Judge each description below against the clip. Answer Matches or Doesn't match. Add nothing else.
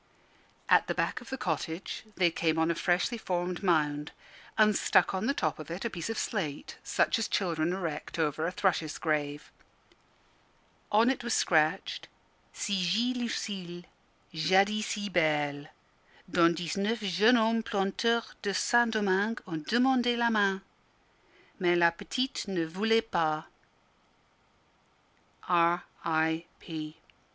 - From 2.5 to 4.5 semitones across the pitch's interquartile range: Doesn't match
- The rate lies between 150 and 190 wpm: Doesn't match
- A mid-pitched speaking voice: Matches